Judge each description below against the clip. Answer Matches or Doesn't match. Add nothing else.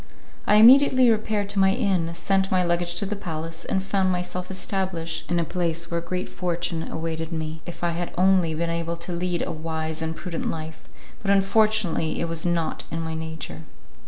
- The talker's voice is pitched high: Doesn't match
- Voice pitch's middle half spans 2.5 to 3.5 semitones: Matches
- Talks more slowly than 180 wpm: Doesn't match